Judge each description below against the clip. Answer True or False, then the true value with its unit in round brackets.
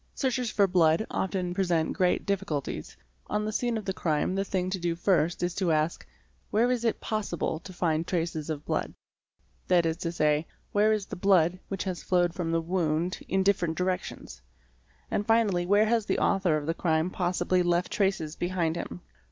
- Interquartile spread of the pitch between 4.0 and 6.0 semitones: False (3.0 semitones)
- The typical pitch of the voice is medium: True (180 Hz)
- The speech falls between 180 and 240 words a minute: True (190 wpm)